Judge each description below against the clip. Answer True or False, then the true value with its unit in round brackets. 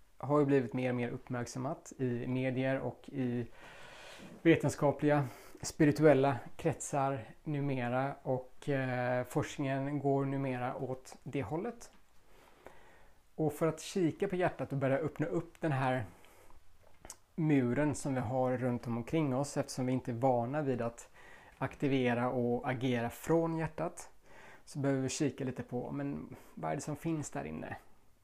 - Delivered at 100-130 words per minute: False (145 wpm)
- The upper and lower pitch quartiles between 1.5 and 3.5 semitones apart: True (2.8 semitones)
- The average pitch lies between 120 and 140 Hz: True (135 Hz)